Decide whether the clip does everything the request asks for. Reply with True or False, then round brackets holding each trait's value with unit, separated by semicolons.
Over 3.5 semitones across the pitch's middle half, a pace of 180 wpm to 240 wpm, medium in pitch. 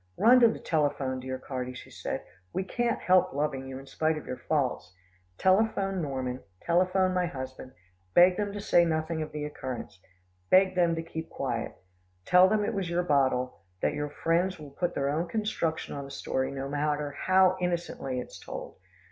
True (5.2 semitones; 190 wpm; 160 Hz)